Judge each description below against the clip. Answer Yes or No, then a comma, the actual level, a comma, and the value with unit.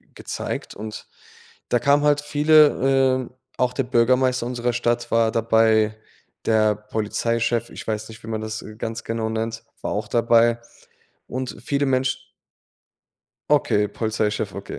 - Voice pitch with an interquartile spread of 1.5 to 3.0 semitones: Yes, average, 2.7 semitones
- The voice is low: Yes, low, 115 Hz